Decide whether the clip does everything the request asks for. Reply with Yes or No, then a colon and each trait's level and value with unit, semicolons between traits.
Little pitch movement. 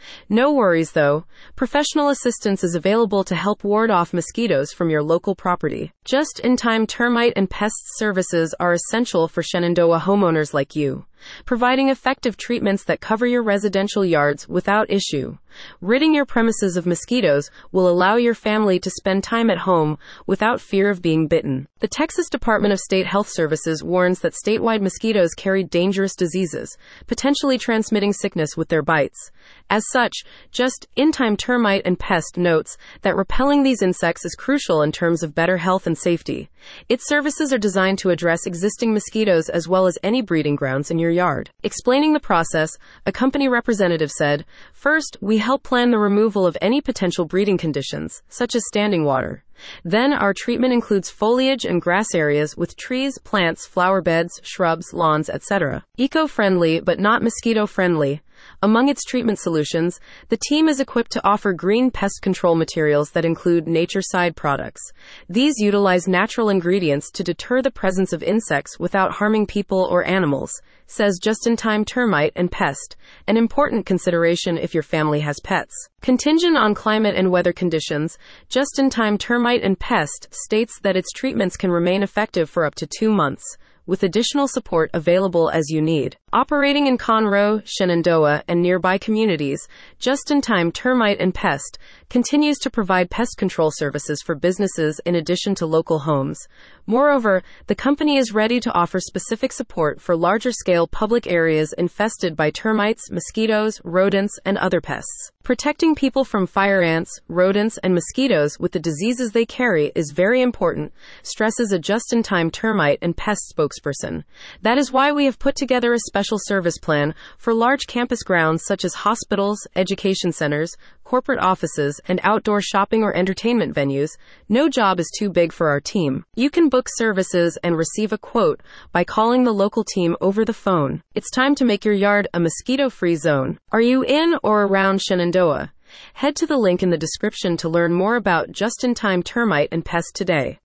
No: wide, 5.4 semitones